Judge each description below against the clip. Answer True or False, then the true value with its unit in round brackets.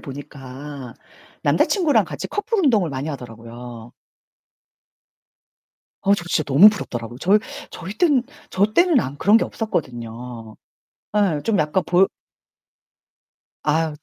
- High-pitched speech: False (150 Hz)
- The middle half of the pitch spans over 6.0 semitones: True (8.7 semitones)